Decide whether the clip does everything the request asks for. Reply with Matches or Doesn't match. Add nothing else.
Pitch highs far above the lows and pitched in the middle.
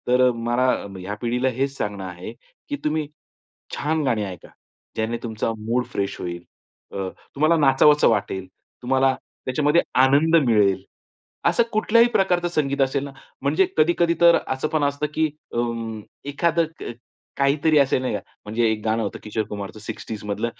Doesn't match